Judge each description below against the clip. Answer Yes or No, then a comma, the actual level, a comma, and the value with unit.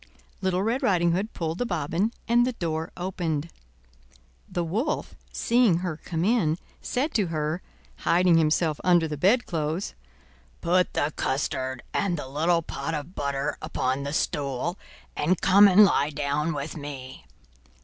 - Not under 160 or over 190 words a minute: No, average, 150 wpm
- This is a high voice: No, medium, 165 Hz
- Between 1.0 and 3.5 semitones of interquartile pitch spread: No, average, 3.9 semitones